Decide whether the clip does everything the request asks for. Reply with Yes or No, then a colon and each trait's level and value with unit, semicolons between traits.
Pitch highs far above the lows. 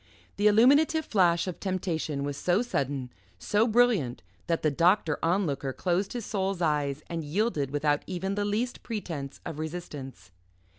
Yes: wide, 5.9 semitones